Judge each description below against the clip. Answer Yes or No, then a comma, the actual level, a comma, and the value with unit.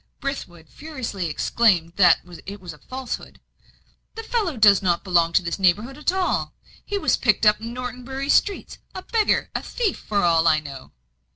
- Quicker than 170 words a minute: Yes, average, 180 wpm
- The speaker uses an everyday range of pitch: No, wide, 7.9 semitones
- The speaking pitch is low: No, high, 215 Hz